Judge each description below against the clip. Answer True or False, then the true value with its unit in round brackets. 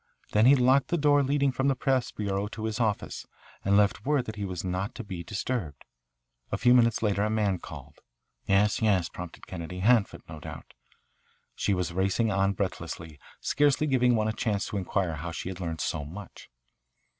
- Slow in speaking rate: False (190 wpm)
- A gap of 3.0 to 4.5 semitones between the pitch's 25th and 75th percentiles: False (5.0 semitones)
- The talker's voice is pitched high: False (105 Hz)